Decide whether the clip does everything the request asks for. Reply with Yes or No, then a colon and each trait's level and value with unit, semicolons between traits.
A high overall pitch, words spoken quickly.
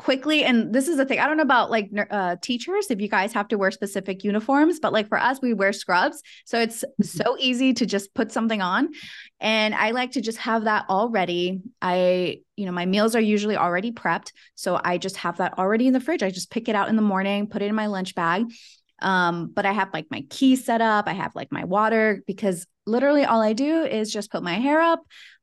Yes: high, 215 Hz; fast, 240 wpm